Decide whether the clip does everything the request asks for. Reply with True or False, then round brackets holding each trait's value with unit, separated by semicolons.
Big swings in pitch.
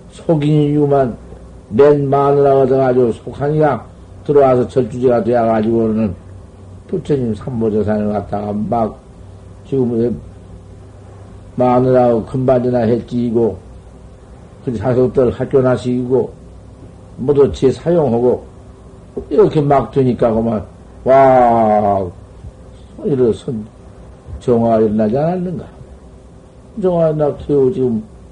False (5.0 semitones)